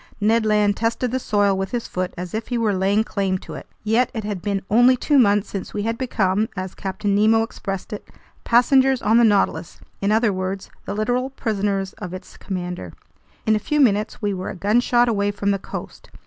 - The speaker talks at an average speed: No, fast, 210 wpm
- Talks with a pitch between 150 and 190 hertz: No, high, 210 Hz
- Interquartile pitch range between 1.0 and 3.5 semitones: Yes, average, 2.9 semitones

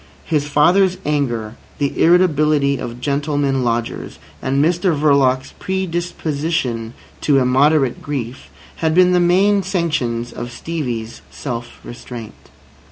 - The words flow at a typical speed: No, slow, 110 wpm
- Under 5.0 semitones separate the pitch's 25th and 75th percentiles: No, average, 5.3 semitones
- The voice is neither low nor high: Yes, medium, 145 Hz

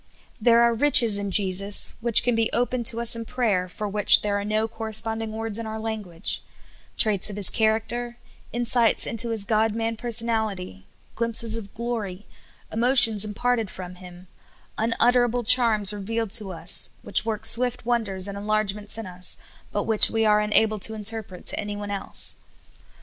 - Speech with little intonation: Yes, narrow, 2.2 semitones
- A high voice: Yes, high, 220 Hz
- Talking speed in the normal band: Yes, average, 170 wpm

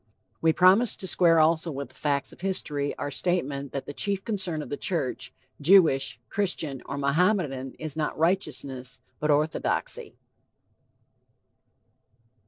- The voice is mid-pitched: Yes, medium, 155 Hz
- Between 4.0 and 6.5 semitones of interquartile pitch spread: Yes, average, 4.6 semitones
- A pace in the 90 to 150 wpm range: Yes, slow, 135 wpm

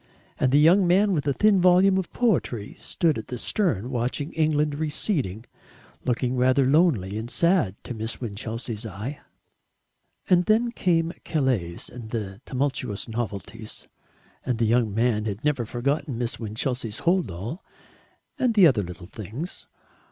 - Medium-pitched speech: No, low, 130 Hz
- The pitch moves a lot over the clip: Yes, wide, 6.8 semitones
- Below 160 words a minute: Yes, average, 145 wpm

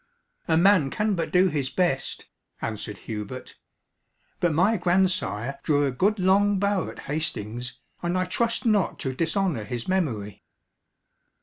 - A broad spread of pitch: Yes, wide, 6.9 semitones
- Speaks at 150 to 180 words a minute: No, average, 140 wpm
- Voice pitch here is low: No, medium, 170 Hz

